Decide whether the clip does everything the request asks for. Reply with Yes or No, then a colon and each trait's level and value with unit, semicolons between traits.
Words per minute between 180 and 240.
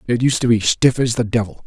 No: fast, 290 wpm